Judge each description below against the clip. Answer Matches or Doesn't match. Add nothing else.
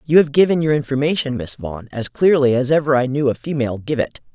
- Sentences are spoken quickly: Matches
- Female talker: Matches